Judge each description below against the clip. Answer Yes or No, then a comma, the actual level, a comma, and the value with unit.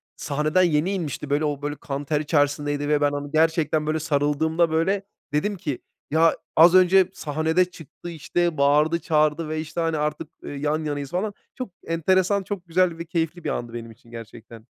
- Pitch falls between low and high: Yes, medium, 155 Hz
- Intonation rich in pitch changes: No, average, 2.8 semitones